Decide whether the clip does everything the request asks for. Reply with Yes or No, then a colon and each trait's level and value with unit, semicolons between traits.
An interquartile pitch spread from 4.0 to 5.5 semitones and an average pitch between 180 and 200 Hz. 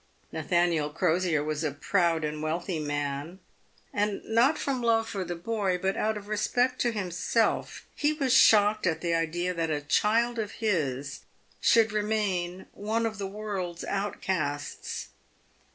Yes: average, 5.0 semitones; high, 190 Hz